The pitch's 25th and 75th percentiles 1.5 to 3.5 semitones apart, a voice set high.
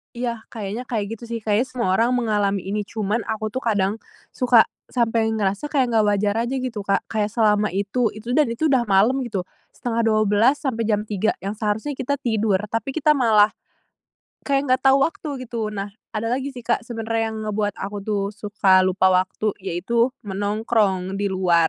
Yes: average, 2.9 semitones; high, 220 Hz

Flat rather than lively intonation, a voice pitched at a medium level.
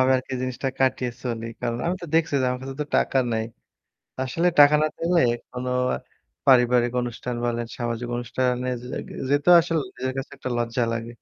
No: narrow, 2.0 semitones; low, 125 Hz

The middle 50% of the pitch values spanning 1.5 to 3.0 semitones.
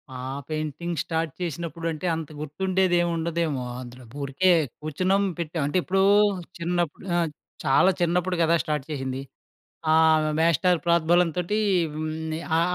Yes: narrow, 2.4 semitones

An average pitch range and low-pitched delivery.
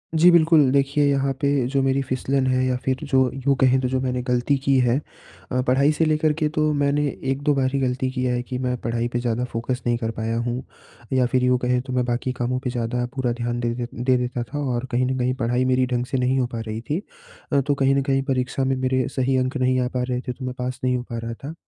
No: narrow, 1.6 semitones; low, 130 Hz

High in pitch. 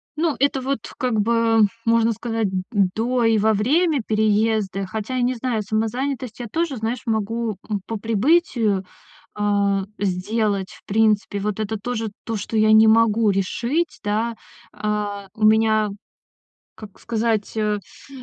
Yes: high, 220 Hz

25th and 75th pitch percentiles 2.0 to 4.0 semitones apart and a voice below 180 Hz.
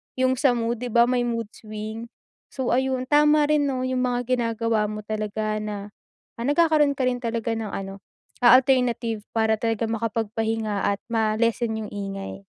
No: average, 2.8 semitones; high, 230 Hz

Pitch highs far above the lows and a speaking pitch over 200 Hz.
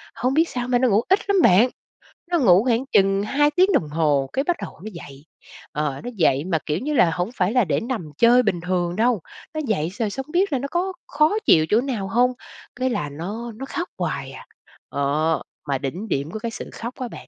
Yes: wide, 7.6 semitones; high, 220 Hz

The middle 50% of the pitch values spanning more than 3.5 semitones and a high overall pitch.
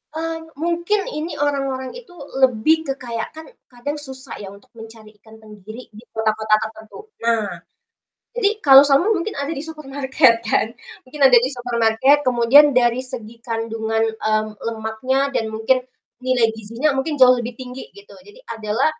Yes: average, 4.1 semitones; high, 245 Hz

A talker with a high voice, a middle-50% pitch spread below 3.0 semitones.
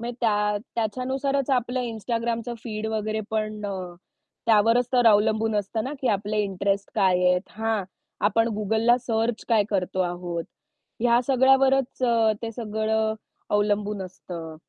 Yes: high, 220 Hz; narrow, 2.5 semitones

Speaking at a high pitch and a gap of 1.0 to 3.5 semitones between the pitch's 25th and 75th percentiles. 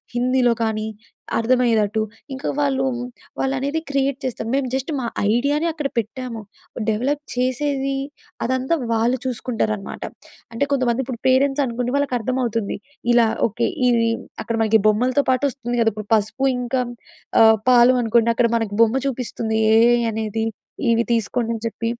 Yes: high, 245 Hz; average, 2.7 semitones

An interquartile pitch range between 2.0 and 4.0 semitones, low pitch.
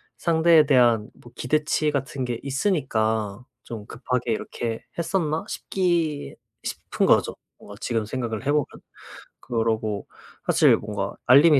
No: average, 5.2 semitones; low, 130 Hz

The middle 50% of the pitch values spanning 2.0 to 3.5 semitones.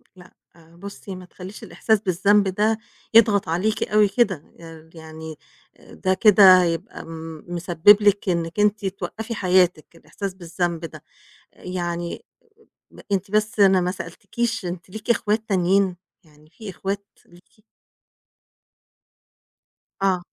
Yes: average, 3.2 semitones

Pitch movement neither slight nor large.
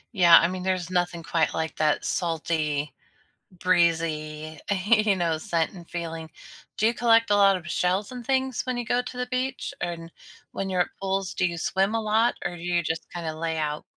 Yes: average, 4.1 semitones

